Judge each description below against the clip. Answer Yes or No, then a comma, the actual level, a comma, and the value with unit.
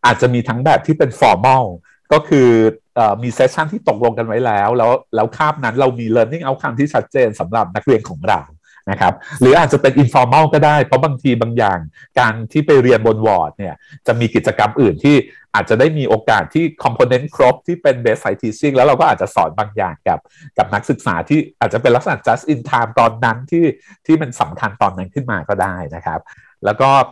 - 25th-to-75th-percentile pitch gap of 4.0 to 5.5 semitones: Yes, average, 4.6 semitones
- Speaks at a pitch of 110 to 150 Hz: Yes, low, 135 Hz